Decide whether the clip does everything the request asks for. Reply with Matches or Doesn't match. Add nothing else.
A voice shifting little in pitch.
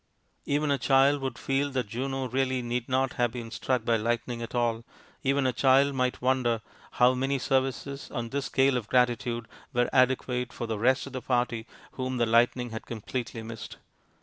Matches